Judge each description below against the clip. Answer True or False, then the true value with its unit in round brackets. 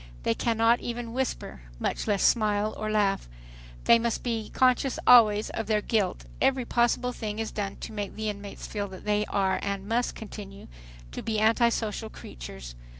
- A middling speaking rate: True (170 wpm)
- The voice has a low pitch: False (215 Hz)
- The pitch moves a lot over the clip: False (2.4 semitones)